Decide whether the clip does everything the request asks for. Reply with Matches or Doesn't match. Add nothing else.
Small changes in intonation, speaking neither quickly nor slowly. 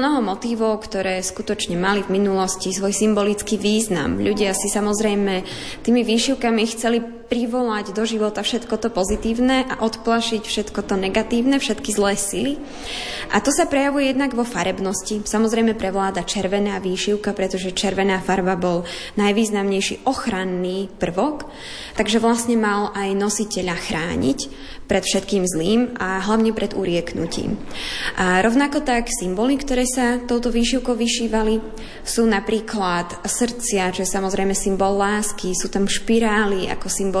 Doesn't match